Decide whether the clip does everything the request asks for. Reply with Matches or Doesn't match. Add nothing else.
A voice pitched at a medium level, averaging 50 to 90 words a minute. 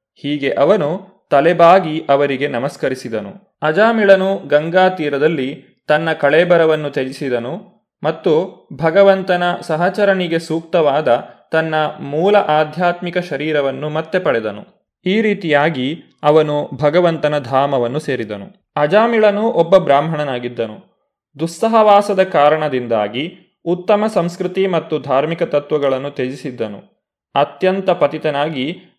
Matches